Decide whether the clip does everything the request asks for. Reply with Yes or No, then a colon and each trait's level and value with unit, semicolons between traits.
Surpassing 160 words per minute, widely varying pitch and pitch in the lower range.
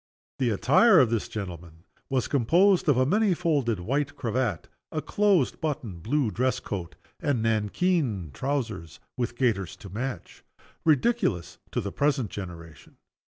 No: average, 140 wpm; wide, 6.7 semitones; low, 125 Hz